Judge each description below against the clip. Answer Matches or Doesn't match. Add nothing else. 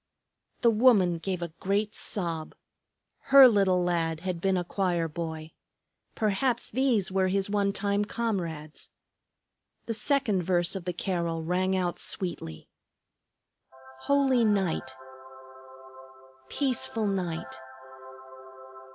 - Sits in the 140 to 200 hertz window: Matches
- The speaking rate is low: Matches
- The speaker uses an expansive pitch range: Doesn't match